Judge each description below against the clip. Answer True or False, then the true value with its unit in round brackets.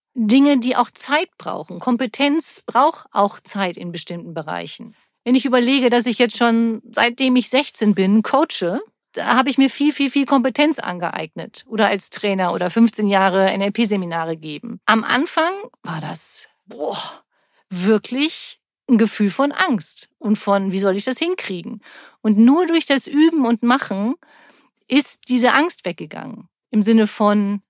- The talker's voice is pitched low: False (235 Hz)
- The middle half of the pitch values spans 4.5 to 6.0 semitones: True (5.2 semitones)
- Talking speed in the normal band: True (155 wpm)